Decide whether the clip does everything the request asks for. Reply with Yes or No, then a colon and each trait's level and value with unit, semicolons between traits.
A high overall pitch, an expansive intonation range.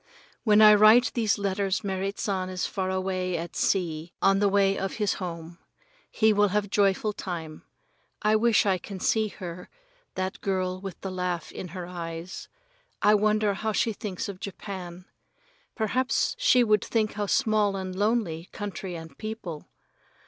No: high, 195 Hz; narrow, 2.6 semitones